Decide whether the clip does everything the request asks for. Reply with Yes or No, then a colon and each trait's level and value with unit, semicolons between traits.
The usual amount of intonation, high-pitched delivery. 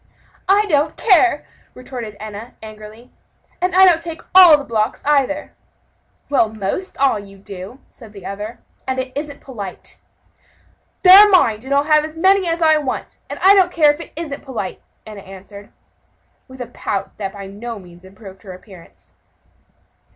No: wide, 7.5 semitones; very high, 255 Hz